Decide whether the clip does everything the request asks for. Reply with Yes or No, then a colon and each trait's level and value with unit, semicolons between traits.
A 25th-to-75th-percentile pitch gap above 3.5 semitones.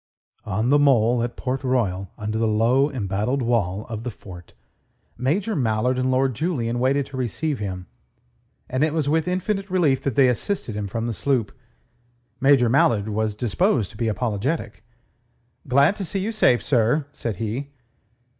Yes: average, 4.5 semitones